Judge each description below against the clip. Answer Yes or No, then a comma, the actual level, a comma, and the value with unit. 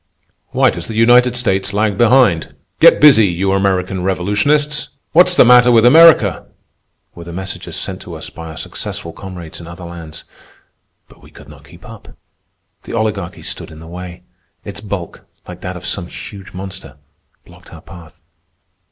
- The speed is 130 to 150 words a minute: No, average, 165 wpm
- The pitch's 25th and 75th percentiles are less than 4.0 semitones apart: No, average, 4.7 semitones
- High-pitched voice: No, very low, 95 Hz